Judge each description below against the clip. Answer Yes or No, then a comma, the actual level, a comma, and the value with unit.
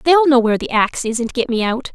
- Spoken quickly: Yes, fast, 310 wpm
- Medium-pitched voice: No, very high, 250 Hz